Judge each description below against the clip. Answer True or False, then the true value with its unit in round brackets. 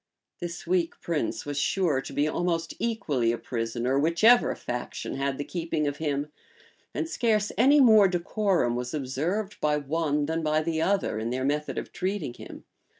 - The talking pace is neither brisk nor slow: True (170 wpm)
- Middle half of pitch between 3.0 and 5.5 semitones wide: True (4.9 semitones)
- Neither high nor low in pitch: True (155 Hz)